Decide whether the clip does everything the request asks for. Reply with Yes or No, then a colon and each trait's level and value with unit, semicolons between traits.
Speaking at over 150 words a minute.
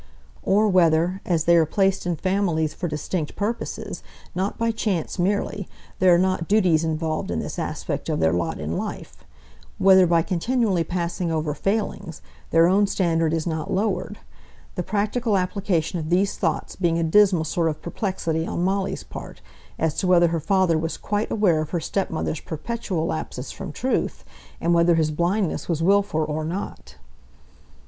Yes: average, 170 wpm